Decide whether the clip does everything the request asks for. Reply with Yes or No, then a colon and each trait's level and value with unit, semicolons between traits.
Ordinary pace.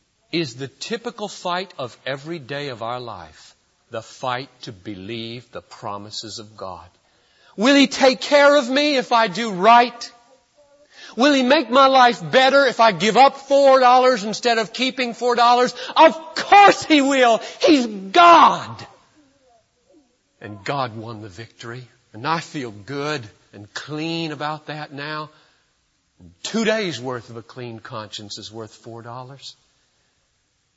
Yes: average, 150 wpm